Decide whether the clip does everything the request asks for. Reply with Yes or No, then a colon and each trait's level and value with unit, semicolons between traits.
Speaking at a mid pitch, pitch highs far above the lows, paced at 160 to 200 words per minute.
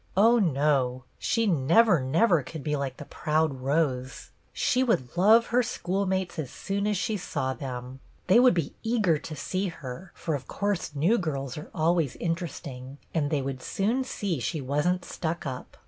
Yes: medium, 160 Hz; wide, 6.2 semitones; average, 180 wpm